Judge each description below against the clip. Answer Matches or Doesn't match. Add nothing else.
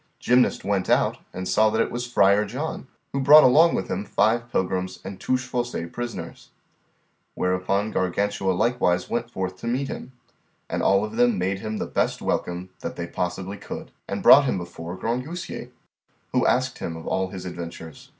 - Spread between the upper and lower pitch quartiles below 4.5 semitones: Doesn't match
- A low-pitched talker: Matches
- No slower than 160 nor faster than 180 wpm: Matches